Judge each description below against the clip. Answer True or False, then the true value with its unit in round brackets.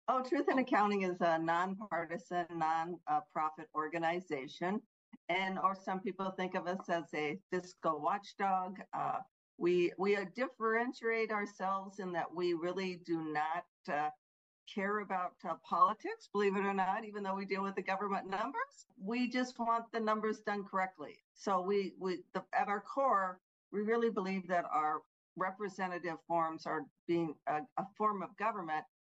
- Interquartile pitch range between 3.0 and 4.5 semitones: True (3.7 semitones)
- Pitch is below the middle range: False (190 Hz)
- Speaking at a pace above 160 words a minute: False (155 wpm)